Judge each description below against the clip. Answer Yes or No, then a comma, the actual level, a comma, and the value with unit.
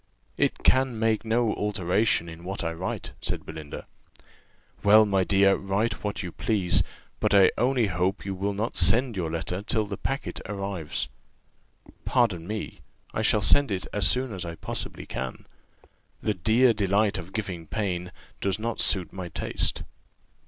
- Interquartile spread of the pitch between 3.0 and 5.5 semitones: Yes, average, 3.3 semitones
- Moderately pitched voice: No, low, 100 Hz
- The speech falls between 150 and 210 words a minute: Yes, average, 160 wpm